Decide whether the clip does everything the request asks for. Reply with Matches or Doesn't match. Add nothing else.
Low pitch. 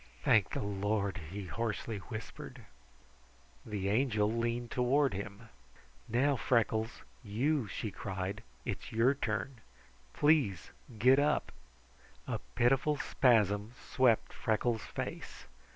Matches